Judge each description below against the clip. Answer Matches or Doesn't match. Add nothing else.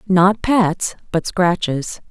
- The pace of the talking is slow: Matches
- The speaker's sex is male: Doesn't match